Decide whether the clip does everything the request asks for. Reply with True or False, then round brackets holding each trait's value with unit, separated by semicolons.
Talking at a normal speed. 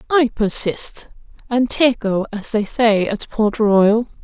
False (115 wpm)